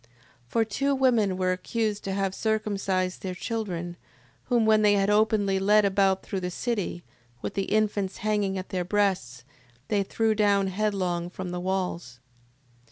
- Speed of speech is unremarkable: Yes, average, 165 wpm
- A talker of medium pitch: No, high, 195 Hz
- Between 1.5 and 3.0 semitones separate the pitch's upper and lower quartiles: Yes, narrow, 2.5 semitones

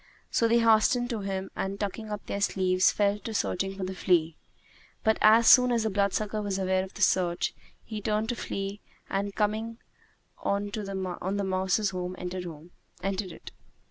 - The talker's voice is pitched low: No, high, 200 Hz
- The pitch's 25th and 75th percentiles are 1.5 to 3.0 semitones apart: Yes, narrow, 2.4 semitones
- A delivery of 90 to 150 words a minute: No, average, 170 wpm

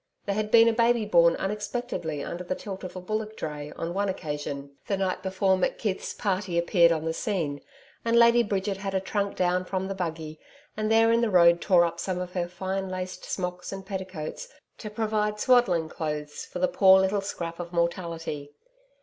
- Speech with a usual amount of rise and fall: Yes, average, 3.3 semitones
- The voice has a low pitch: No, medium, 185 Hz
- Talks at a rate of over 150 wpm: Yes, average, 195 wpm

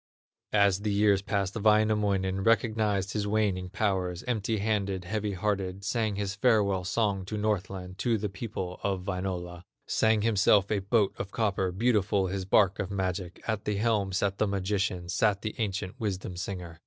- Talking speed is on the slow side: No, average, 165 wpm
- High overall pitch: No, low, 100 Hz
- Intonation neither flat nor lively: No, narrow, 2.2 semitones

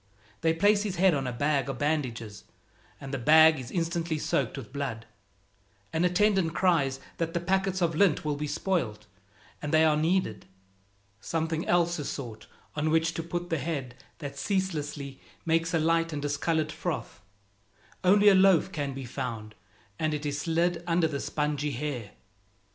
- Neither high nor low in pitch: Yes, medium, 155 Hz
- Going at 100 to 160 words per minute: No, average, 170 wpm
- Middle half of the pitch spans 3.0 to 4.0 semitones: Yes, average, 3.4 semitones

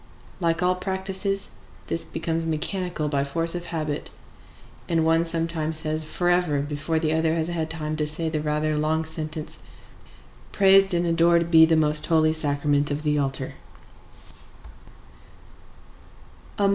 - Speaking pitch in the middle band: Yes, medium, 160 Hz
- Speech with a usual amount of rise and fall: No, narrow, 1.7 semitones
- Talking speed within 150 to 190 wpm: No, slow, 135 wpm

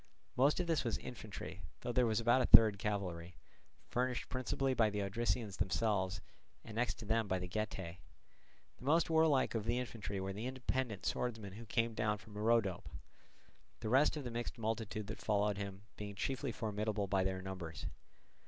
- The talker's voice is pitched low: Yes, low, 110 Hz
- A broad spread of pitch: No, average, 3.5 semitones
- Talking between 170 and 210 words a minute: Yes, average, 180 wpm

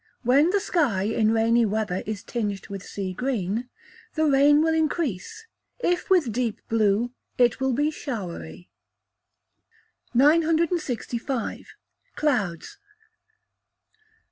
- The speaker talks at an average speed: No, slow, 105 wpm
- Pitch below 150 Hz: No, high, 245 Hz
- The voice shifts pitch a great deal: Yes, wide, 6.3 semitones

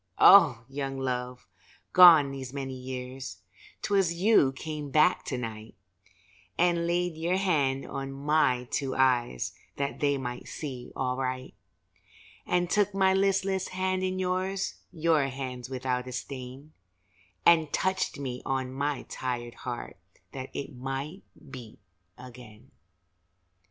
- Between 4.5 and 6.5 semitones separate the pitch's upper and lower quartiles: Yes, average, 5.1 semitones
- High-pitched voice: No, low, 135 Hz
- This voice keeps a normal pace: No, slow, 125 wpm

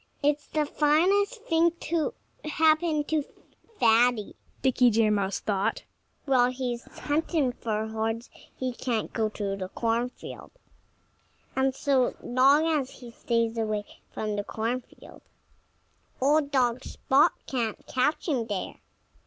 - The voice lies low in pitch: No, very high, 250 Hz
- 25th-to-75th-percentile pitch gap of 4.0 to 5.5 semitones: Yes, average, 4.8 semitones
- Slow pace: Yes, slow, 130 wpm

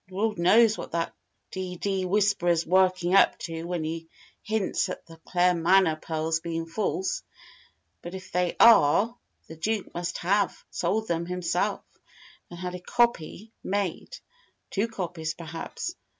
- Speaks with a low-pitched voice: No, medium, 180 Hz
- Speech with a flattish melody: No, average, 3.2 semitones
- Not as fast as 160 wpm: Yes, average, 140 wpm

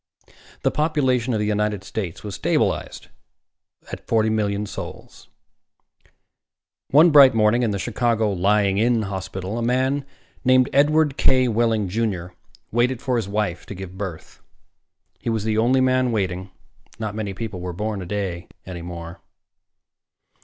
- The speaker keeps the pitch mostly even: No, average, 4.1 semitones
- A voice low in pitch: Yes, low, 110 Hz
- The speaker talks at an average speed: Yes, average, 145 wpm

